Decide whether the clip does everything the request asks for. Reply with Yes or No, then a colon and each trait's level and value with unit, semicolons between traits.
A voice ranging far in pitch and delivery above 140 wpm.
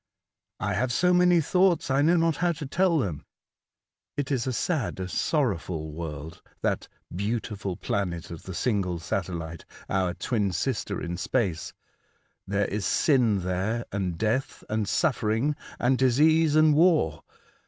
Yes: wide, 8.2 semitones; average, 155 wpm